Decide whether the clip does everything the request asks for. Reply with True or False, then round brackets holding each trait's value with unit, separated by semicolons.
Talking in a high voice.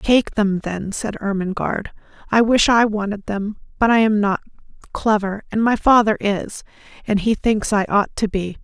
True (210 Hz)